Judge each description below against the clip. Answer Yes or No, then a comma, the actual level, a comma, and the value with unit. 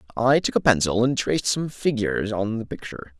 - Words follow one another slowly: No, fast, 205 wpm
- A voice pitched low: Yes, low, 115 Hz